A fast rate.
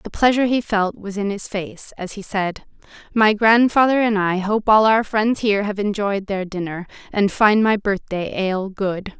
No: average, 195 wpm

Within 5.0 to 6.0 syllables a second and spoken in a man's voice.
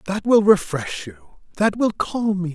No: 4.5 syllables/s; male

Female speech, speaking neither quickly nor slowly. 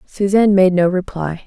Yes: female; average, 165 wpm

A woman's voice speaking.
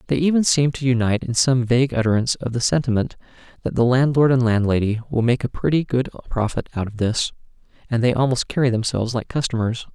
No: male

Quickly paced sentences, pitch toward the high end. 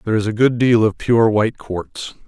No: fast, 240 wpm; low, 110 Hz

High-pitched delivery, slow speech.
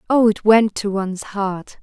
No: high, 205 Hz; average, 200 wpm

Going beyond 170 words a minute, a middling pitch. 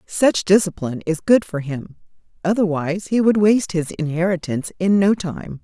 No: average, 160 wpm; medium, 180 Hz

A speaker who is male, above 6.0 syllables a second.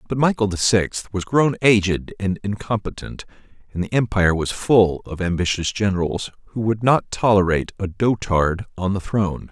No: male; 5.1 syllables/s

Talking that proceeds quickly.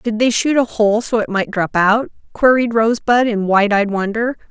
Yes: fast, 215 wpm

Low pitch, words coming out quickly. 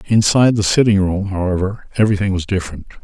No: low, 100 Hz; average, 160 wpm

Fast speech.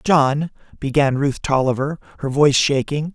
No: slow, 135 wpm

